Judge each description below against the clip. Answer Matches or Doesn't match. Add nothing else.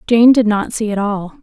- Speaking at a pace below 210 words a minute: Doesn't match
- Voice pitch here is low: Doesn't match